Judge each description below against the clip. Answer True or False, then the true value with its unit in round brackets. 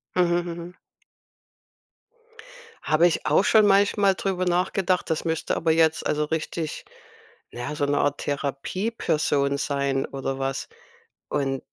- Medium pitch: True (160 Hz)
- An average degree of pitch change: True (4.2 semitones)